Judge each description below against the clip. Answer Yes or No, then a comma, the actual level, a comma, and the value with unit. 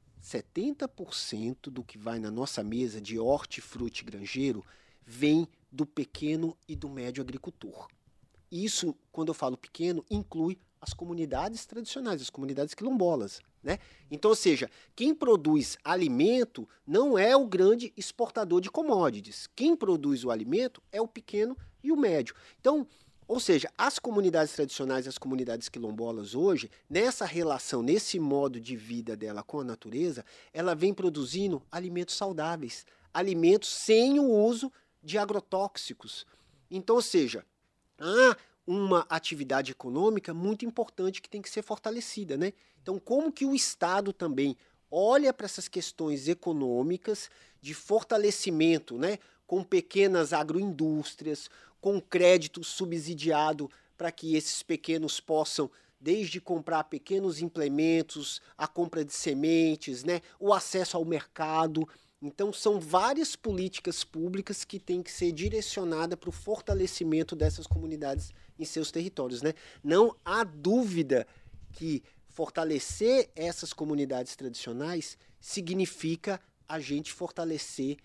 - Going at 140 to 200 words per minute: No, average, 130 wpm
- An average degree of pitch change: No, wide, 5.8 semitones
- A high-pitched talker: No, medium, 170 Hz